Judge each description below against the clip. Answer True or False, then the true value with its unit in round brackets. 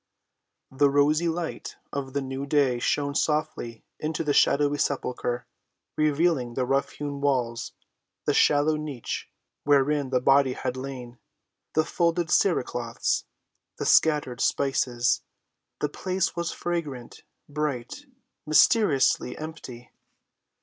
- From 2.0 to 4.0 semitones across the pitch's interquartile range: True (3.2 semitones)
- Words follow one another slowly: True (110 wpm)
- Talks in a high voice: False (140 Hz)